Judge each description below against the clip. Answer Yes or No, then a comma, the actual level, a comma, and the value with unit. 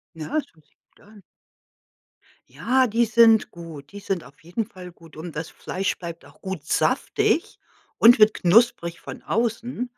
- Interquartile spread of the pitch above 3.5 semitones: Yes, wide, 5.5 semitones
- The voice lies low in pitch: No, high, 200 Hz